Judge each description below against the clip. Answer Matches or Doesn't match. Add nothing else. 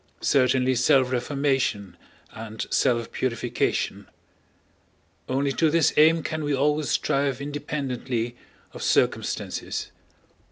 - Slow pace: Matches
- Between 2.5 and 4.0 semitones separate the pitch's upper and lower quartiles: Matches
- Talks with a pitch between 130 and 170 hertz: Matches